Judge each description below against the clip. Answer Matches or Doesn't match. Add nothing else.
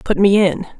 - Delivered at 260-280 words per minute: Doesn't match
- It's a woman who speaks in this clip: Matches